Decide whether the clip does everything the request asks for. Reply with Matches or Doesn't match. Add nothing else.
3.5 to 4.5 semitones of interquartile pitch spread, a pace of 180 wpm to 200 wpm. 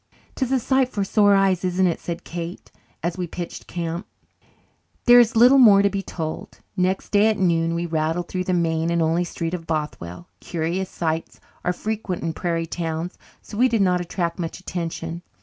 Doesn't match